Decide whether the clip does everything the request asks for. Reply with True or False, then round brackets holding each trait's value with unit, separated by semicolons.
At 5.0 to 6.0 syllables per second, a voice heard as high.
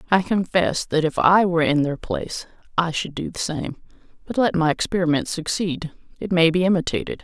False (5.5 syllables/s; 170 Hz)